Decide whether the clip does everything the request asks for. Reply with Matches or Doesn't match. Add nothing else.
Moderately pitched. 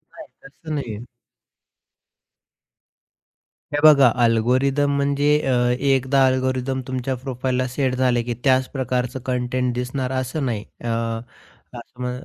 Doesn't match